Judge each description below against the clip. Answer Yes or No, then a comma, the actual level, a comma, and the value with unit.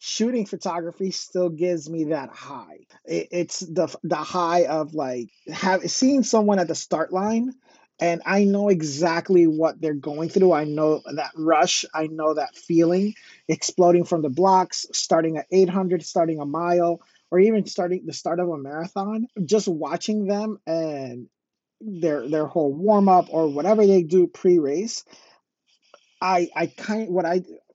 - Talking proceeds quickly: No, average, 165 wpm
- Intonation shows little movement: No, average, 3.3 semitones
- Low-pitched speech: No, medium, 175 Hz